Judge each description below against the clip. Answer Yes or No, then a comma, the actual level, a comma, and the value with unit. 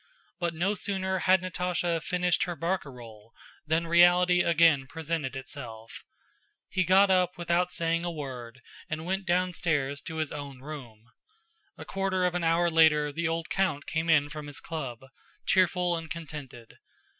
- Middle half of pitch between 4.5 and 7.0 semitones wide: No, average, 3.7 semitones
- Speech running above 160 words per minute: No, average, 155 wpm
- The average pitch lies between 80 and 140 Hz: No, medium, 165 Hz